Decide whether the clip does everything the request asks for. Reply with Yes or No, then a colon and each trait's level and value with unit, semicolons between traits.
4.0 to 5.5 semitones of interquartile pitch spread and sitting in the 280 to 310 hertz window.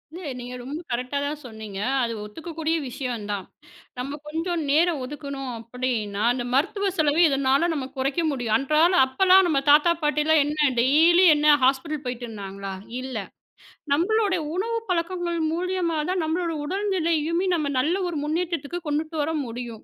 Yes: average, 4.9 semitones; very high, 300 Hz